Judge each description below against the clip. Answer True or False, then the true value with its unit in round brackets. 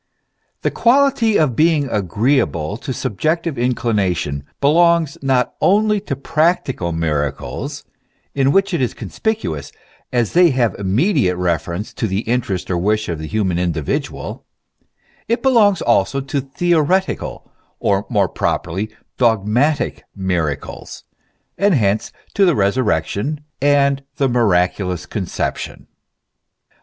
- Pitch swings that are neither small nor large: False (8.5 semitones)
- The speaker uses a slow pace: True (120 wpm)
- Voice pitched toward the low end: True (120 Hz)